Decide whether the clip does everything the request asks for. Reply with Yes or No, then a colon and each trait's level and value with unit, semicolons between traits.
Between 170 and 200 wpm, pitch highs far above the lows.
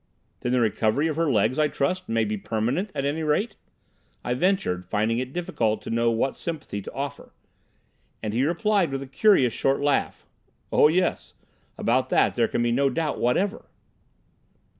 Yes: average, 175 wpm; wide, 5.9 semitones